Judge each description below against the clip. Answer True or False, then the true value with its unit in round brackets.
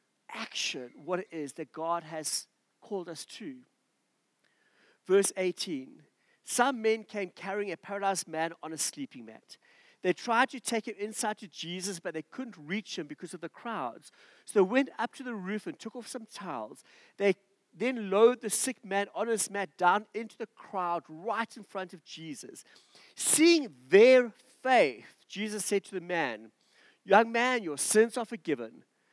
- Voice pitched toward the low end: False (205 Hz)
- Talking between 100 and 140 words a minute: False (175 wpm)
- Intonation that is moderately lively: True (4.7 semitones)